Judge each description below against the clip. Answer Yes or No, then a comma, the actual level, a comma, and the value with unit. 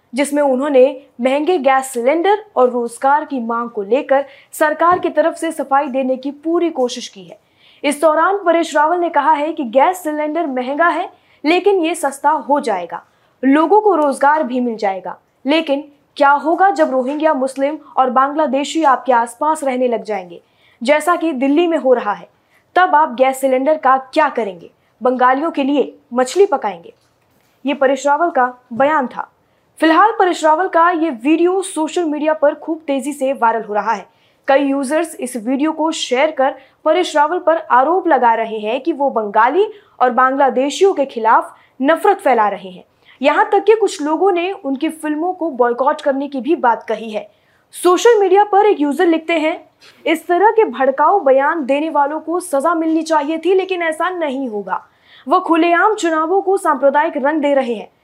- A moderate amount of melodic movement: Yes, average, 4.0 semitones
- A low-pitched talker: No, very high, 295 Hz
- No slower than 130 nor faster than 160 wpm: No, average, 180 wpm